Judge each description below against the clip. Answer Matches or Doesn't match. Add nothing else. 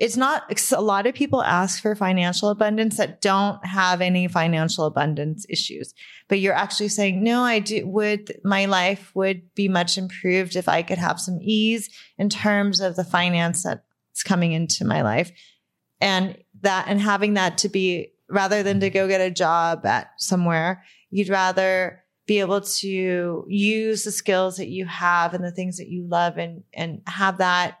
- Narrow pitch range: Matches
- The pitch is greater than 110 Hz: Matches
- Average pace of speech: Matches